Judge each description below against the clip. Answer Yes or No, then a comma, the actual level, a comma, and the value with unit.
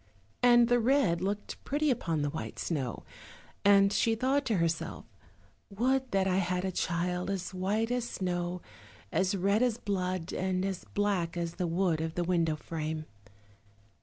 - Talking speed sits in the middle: Yes, average, 165 wpm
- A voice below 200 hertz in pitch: Yes, medium, 185 Hz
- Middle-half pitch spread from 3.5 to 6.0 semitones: Yes, average, 4.0 semitones